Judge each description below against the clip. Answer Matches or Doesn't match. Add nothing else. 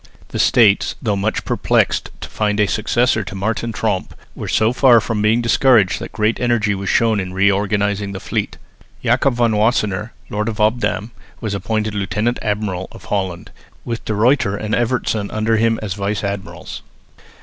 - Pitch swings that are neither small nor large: Doesn't match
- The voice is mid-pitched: Doesn't match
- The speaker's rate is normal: Matches